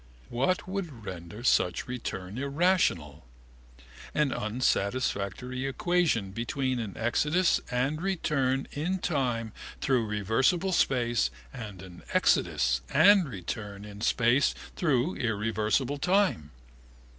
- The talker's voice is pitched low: Yes, low, 125 Hz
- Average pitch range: No, wide, 6.3 semitones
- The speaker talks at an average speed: No, slow, 100 wpm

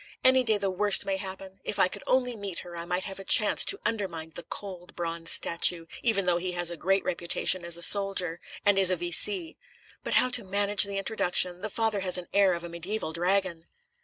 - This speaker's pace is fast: Yes, fast, 220 wpm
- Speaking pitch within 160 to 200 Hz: Yes, high, 190 Hz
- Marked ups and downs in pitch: No, average, 2.7 semitones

